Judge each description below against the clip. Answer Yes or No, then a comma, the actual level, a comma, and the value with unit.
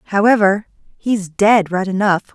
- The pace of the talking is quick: No, slow, 130 wpm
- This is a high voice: Yes, high, 200 Hz